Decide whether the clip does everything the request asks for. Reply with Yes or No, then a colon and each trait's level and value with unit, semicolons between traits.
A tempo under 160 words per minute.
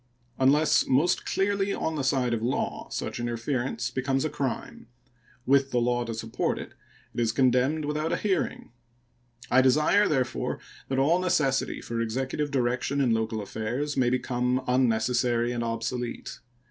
Yes: average, 150 wpm